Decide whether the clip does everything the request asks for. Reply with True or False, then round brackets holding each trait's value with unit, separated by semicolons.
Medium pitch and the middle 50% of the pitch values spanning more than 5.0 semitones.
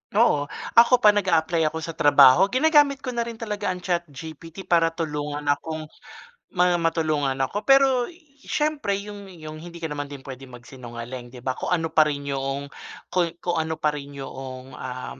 True (160 Hz; 5.6 semitones)